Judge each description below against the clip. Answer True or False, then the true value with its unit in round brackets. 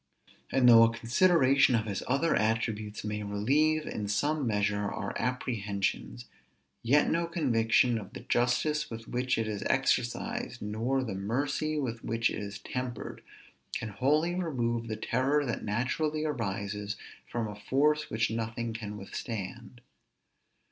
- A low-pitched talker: True (115 Hz)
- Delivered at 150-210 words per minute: False (140 wpm)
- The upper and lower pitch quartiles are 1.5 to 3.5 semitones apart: False (4.4 semitones)